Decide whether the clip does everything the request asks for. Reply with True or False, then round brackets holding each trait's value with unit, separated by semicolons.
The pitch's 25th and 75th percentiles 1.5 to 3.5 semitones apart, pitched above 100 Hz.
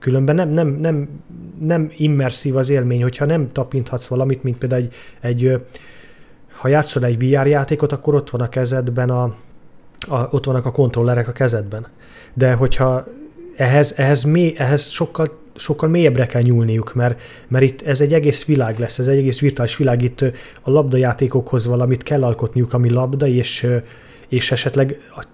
True (2.9 semitones; 130 Hz)